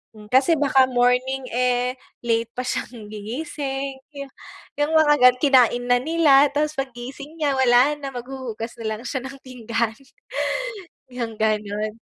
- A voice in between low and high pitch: No, very high, 250 Hz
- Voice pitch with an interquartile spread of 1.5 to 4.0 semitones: Yes, average, 2.7 semitones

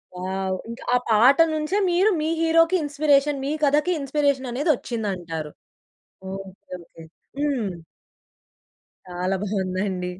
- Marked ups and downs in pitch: Yes, wide, 7.6 semitones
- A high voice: Yes, high, 245 Hz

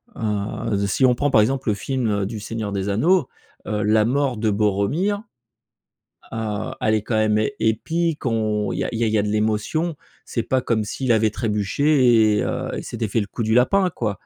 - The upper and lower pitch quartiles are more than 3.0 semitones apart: Yes, average, 3.5 semitones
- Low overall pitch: Yes, low, 110 Hz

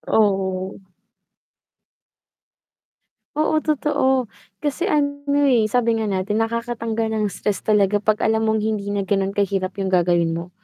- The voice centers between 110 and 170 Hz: No, high, 215 Hz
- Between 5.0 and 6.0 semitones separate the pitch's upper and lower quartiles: No, average, 3.1 semitones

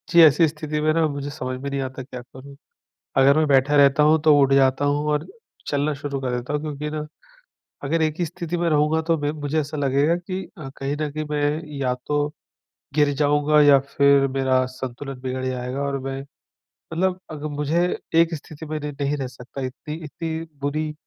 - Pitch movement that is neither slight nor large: No, narrow, 2.0 semitones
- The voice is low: No, medium, 145 Hz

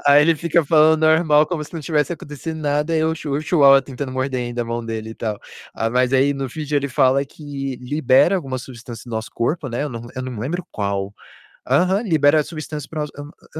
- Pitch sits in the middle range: Yes, medium, 145 Hz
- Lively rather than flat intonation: No, average, 3.7 semitones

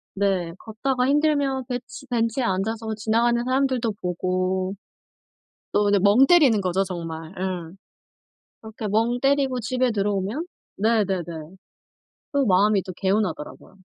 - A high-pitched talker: Yes, high, 220 Hz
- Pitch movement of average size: Yes, average, 4.9 semitones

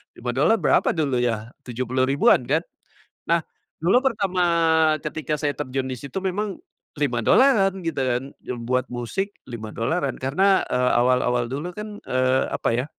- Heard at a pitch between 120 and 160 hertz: Yes, low, 135 Hz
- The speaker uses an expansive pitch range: Yes, wide, 6.4 semitones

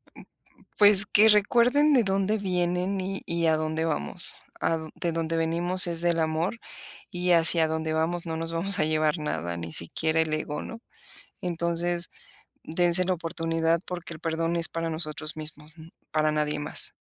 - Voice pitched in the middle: Yes, medium, 165 Hz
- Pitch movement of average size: No, narrow, 2.1 semitones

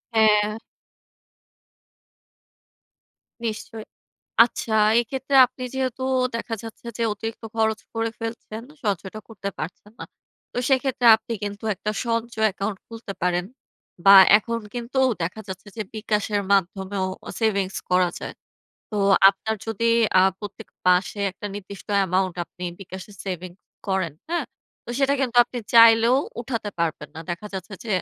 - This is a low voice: No, high, 215 Hz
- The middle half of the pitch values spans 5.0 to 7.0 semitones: No, average, 3.1 semitones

